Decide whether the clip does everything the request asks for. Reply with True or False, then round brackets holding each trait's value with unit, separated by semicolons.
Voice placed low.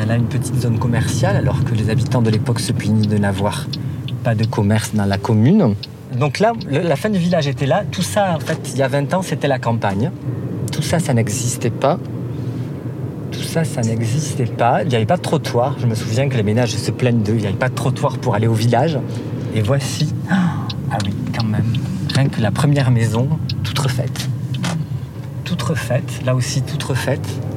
True (130 Hz)